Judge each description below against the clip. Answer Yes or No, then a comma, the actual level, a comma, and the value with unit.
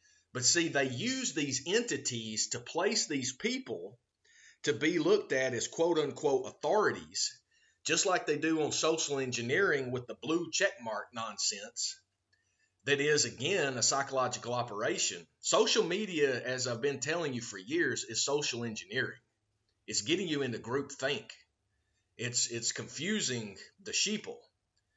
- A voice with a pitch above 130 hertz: Yes, medium, 140 Hz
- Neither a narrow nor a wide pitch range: No, wide, 8.0 semitones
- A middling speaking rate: Yes, average, 145 wpm